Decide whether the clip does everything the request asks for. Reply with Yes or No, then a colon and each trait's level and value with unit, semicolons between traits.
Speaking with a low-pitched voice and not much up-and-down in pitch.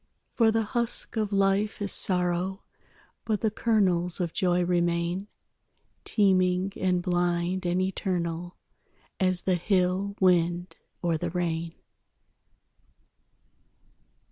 No: medium, 180 Hz; narrow, 2.0 semitones